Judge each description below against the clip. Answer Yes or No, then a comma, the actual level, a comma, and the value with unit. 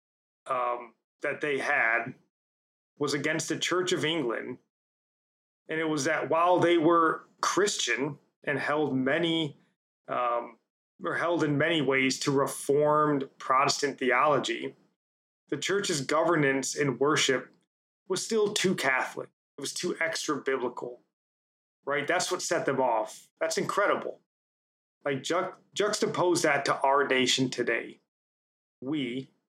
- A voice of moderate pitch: Yes, medium, 150 Hz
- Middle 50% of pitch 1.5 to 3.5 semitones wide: No, average, 4.0 semitones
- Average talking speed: No, slow, 125 wpm